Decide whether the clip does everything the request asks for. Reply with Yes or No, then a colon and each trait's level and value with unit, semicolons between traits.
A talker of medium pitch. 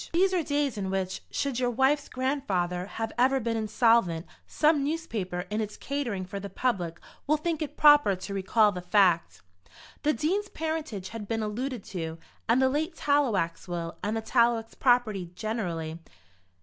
No: high, 225 Hz